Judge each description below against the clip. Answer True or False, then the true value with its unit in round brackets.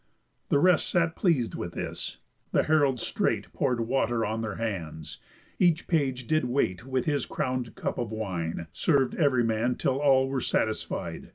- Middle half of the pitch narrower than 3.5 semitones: False (4.1 semitones)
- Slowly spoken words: False (165 wpm)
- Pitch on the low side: True (125 Hz)